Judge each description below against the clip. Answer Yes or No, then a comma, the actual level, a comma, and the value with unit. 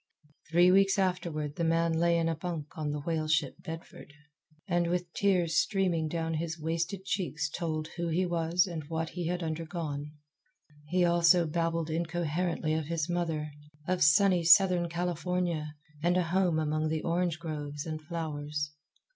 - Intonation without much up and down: Yes, narrow, 2.0 semitones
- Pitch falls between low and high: Yes, medium, 165 Hz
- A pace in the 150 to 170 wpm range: Yes, average, 160 wpm